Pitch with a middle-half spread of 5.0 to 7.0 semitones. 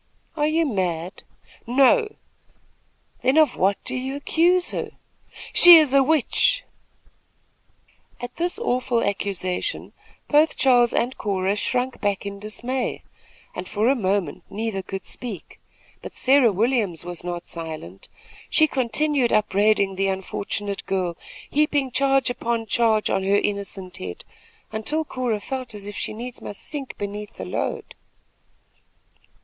Yes: wide, 5.4 semitones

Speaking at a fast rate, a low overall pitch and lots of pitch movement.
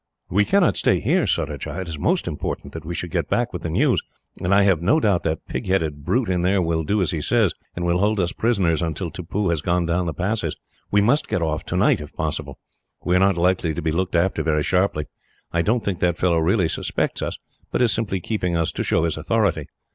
No: fast, 240 wpm; very low, 90 Hz; average, 3.4 semitones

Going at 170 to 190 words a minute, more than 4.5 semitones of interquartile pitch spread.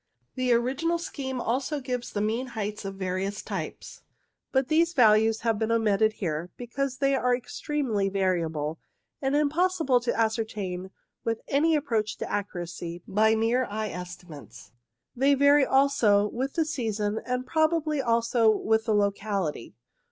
No: average, 150 wpm; average, 4.9 semitones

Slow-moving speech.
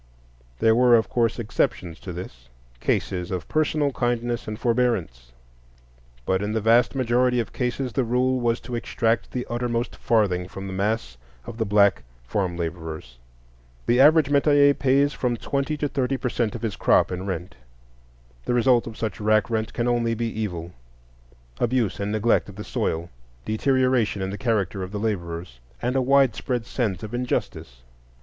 No: average, 165 wpm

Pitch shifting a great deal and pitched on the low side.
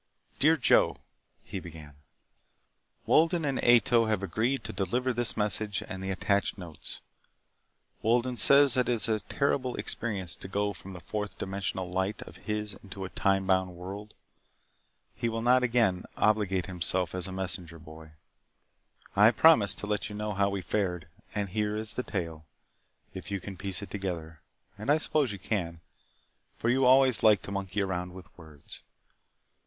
No: average, 3.6 semitones; low, 100 Hz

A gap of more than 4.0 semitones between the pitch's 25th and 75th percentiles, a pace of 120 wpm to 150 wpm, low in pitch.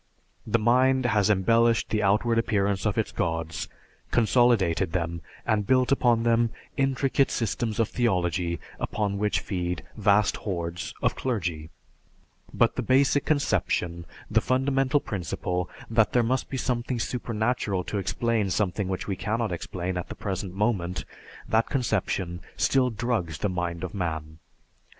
Yes: average, 4.8 semitones; average, 140 wpm; low, 105 Hz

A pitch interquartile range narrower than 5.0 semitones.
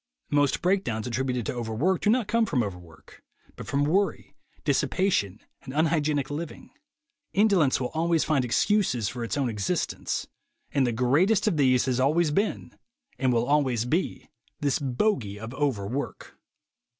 No: wide, 5.6 semitones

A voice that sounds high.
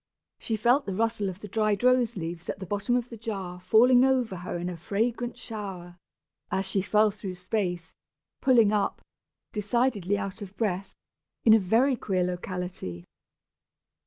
Yes: high, 205 Hz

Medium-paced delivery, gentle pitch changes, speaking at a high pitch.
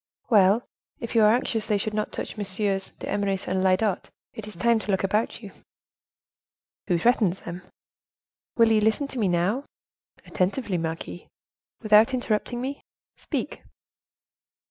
No: average, 145 wpm; average, 3.1 semitones; high, 210 Hz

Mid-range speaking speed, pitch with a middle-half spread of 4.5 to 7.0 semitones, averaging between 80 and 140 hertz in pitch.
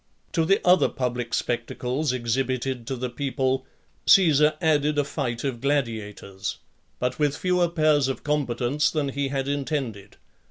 No: average, 145 wpm; average, 3.4 semitones; low, 135 Hz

